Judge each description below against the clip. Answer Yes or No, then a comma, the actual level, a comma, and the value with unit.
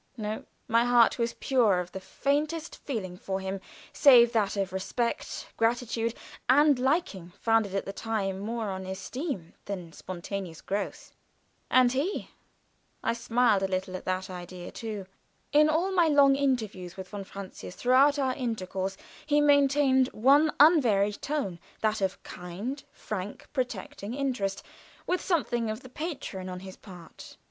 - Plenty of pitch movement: Yes, wide, 6.0 semitones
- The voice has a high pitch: Yes, high, 225 Hz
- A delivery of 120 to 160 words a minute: Yes, average, 145 wpm